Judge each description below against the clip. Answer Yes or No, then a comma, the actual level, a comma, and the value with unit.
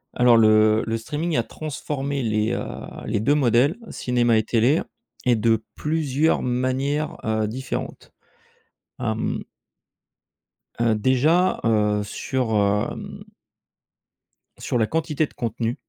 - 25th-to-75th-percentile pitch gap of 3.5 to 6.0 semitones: Yes, average, 4.5 semitones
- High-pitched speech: No, low, 120 Hz